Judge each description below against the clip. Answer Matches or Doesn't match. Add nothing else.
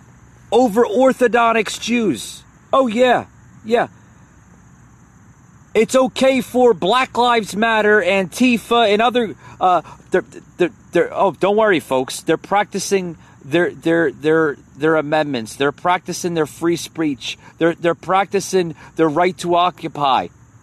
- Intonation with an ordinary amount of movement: Doesn't match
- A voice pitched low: Doesn't match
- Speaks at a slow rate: Matches